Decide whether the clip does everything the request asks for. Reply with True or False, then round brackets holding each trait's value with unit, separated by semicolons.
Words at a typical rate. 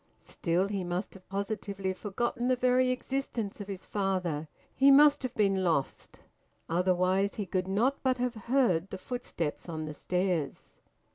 True (155 wpm)